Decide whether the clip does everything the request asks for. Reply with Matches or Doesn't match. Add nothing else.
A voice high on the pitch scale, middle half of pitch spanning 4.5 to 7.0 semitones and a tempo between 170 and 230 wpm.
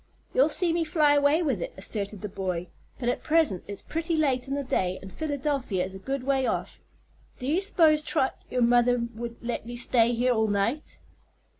Matches